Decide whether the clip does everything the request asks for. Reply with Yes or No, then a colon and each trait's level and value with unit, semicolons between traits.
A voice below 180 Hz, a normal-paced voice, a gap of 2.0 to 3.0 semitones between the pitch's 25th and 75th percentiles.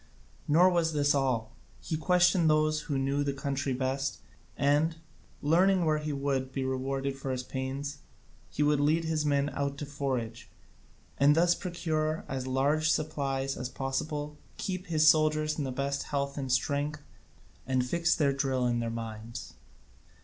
Yes: medium, 140 Hz; average, 165 wpm; narrow, 2.5 semitones